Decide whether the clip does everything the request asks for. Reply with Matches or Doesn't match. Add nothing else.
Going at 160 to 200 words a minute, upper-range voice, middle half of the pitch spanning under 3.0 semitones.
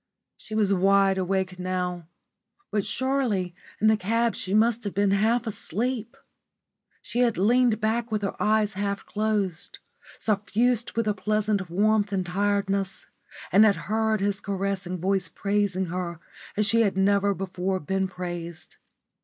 Doesn't match